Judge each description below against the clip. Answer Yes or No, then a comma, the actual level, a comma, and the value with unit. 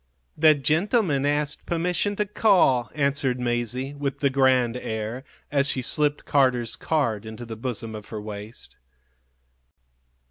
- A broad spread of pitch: No, average, 3.7 semitones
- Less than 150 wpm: Yes, slow, 135 wpm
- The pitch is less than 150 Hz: Yes, low, 135 Hz